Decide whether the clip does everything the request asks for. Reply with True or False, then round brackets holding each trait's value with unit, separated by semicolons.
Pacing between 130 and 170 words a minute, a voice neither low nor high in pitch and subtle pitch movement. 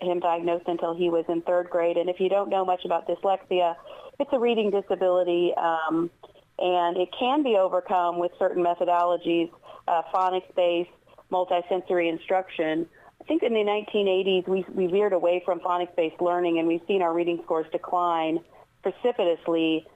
True (160 wpm; 175 Hz; 1.7 semitones)